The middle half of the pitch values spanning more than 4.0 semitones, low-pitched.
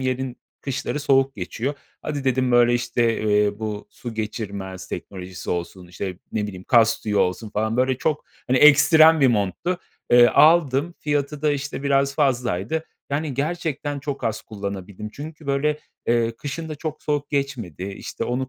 Yes: average, 5.3 semitones; low, 130 Hz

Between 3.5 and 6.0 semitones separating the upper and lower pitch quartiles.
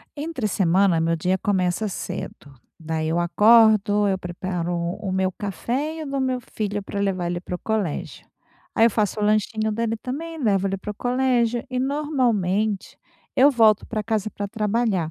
Yes: average, 4.0 semitones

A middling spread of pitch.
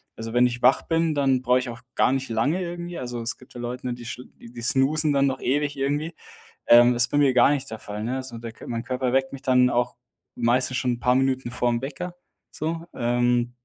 No: narrow, 2.3 semitones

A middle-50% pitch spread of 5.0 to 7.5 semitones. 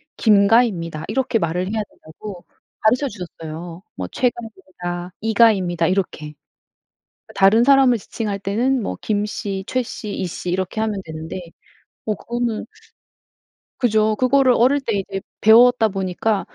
No: average, 4.3 semitones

